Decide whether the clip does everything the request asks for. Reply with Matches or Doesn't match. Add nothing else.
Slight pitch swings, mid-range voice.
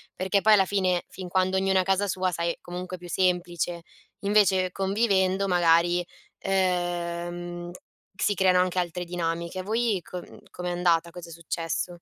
Matches